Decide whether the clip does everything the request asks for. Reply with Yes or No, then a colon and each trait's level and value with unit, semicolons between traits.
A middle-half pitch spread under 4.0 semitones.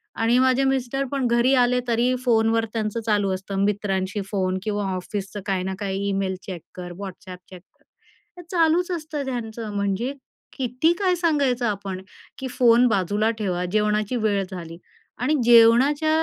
No: average, 4.4 semitones